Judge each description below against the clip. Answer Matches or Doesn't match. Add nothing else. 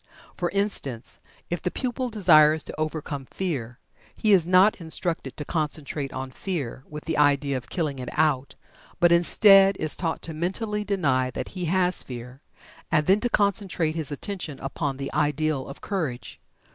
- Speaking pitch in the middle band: Matches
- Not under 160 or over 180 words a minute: Matches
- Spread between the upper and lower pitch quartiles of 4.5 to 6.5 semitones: Matches